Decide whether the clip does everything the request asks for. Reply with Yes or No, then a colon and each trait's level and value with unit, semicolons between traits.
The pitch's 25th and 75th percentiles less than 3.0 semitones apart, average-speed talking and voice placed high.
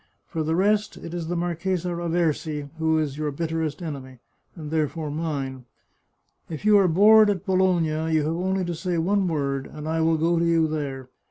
No: narrow, 2.5 semitones; average, 190 wpm; medium, 160 Hz